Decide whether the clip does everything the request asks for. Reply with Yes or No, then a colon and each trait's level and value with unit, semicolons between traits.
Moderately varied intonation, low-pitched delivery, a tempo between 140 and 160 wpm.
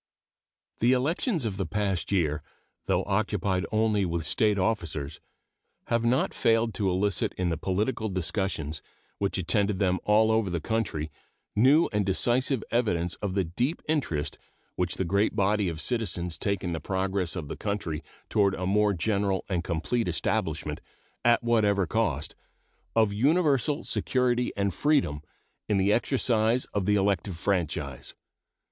Yes: average, 3.9 semitones; low, 100 Hz; average, 150 wpm